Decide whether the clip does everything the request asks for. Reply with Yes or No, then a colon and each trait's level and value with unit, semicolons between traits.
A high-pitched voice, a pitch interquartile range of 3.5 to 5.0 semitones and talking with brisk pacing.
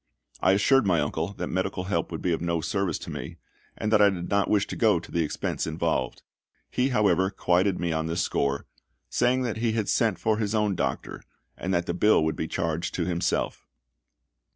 No: very low, 95 Hz; average, 4.1 semitones; fast, 210 wpm